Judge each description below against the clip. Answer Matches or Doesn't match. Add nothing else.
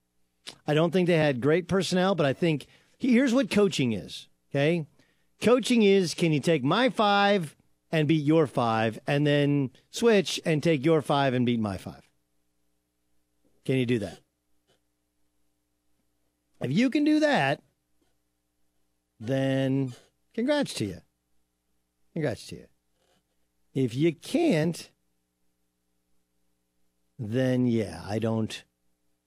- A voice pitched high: Doesn't match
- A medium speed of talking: Doesn't match